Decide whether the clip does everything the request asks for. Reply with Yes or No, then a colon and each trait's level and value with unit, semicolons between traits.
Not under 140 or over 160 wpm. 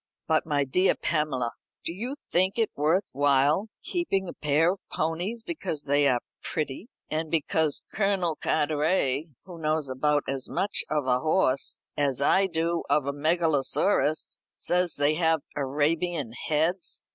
Yes: average, 145 wpm